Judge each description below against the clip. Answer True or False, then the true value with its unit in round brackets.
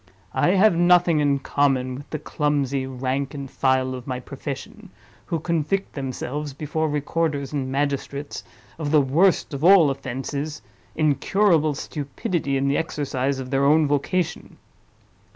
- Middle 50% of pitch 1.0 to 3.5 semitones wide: True (2.6 semitones)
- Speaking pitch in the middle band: True (145 Hz)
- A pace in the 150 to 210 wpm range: False (135 wpm)